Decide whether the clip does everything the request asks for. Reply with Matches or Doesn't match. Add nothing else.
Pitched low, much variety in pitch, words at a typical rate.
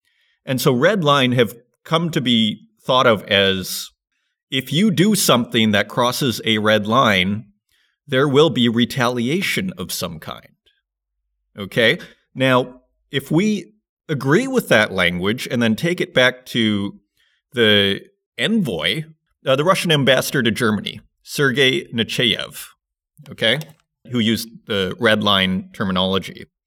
Doesn't match